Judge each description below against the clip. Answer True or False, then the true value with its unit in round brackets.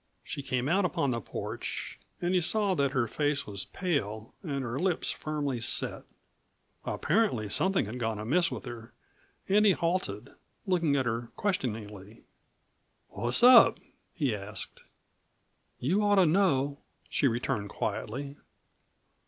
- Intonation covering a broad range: True (7.7 semitones)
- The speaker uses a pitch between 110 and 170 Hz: True (140 Hz)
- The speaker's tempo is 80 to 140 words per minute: True (135 wpm)